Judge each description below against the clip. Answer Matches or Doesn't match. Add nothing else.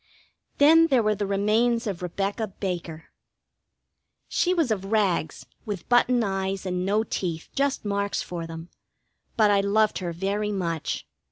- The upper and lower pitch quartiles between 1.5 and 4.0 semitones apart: Matches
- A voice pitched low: Doesn't match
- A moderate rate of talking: Matches